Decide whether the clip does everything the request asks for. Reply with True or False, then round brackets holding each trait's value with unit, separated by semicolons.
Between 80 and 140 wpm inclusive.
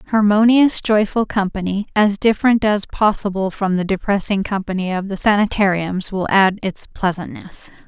True (135 wpm)